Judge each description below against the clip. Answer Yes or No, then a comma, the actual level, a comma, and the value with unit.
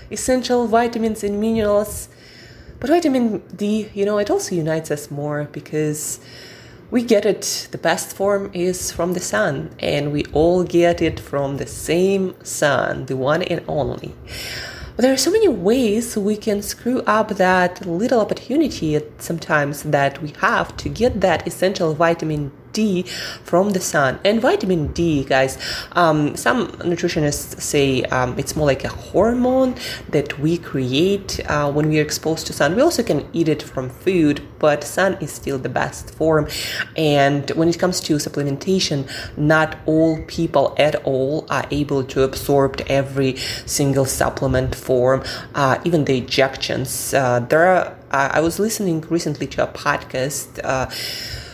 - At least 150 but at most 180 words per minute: Yes, average, 160 wpm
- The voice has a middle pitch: Yes, medium, 155 Hz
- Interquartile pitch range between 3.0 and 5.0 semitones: No, wide, 5.4 semitones